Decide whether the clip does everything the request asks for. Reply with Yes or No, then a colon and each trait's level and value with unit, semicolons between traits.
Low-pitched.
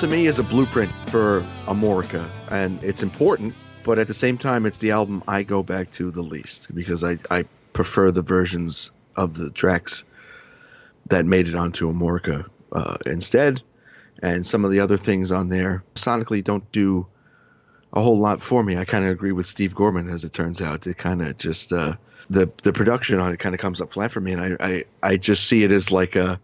Yes: very low, 95 Hz